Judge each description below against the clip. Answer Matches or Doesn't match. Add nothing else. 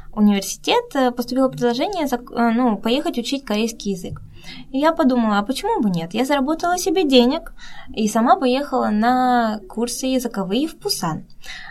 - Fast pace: Doesn't match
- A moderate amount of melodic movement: Matches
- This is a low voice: Doesn't match